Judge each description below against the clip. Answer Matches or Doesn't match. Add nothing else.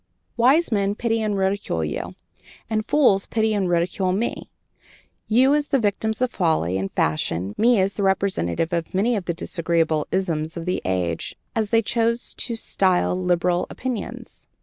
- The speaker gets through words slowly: Doesn't match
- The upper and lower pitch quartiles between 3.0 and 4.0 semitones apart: Doesn't match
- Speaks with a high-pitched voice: Matches